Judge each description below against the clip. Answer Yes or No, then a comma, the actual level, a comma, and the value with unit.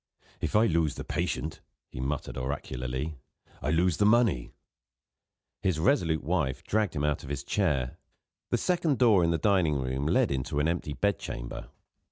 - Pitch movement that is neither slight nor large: No, wide, 6.2 semitones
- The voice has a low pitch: Yes, very low, 80 Hz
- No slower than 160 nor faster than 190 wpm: Yes, average, 170 wpm